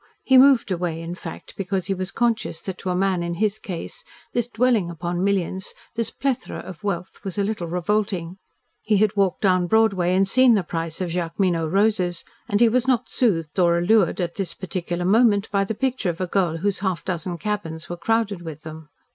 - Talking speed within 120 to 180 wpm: No, fast, 205 wpm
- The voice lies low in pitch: No, high, 190 Hz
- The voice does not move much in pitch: No, average, 3.6 semitones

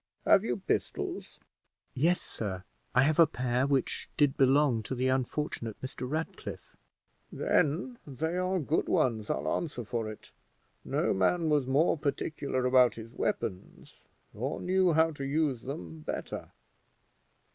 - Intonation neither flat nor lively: Yes, average, 4.5 semitones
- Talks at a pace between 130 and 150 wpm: Yes, average, 140 wpm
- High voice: No, low, 135 Hz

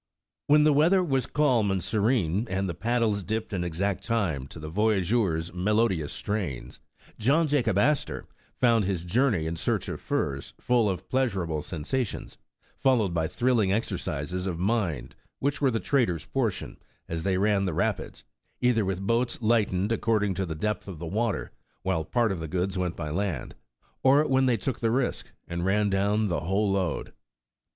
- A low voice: Yes, low, 100 Hz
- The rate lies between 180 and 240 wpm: Yes, average, 185 wpm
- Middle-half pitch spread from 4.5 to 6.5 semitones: Yes, average, 5.1 semitones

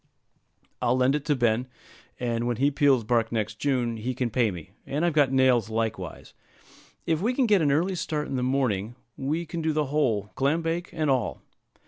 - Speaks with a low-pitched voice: Yes, low, 130 Hz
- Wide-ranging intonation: No, average, 4.6 semitones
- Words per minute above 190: Yes, average, 200 wpm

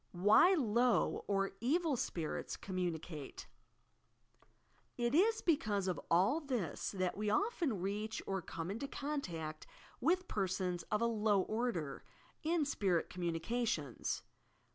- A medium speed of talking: No, slow, 120 wpm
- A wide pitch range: Yes, wide, 7.1 semitones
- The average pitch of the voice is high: Yes, high, 210 Hz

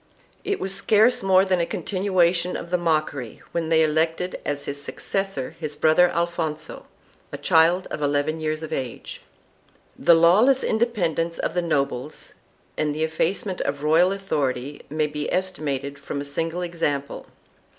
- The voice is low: No, medium, 165 Hz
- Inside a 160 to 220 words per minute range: No, average, 150 wpm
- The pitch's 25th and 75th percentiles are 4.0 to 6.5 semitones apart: No, average, 3.6 semitones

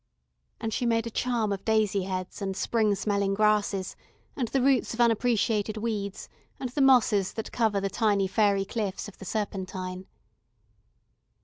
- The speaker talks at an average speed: Yes, average, 155 wpm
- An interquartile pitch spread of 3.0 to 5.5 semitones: No, narrow, 2.5 semitones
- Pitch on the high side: Yes, high, 210 Hz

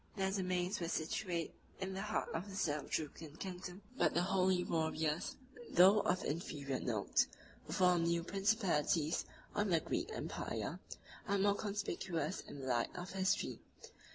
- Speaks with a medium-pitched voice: Yes, medium, 180 Hz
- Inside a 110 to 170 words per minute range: Yes, average, 150 wpm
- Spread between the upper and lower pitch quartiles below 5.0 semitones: Yes, average, 3.3 semitones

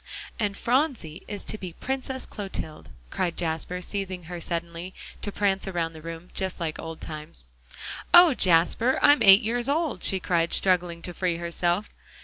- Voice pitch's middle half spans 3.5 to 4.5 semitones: Yes, average, 3.8 semitones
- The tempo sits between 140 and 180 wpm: Yes, average, 160 wpm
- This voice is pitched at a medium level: Yes, medium, 180 Hz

